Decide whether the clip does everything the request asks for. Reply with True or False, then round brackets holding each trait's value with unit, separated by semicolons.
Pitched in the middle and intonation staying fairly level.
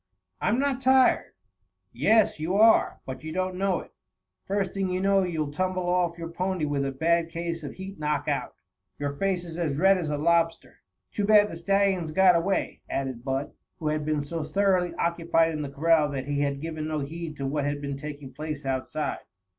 False (165 Hz; 4.0 semitones)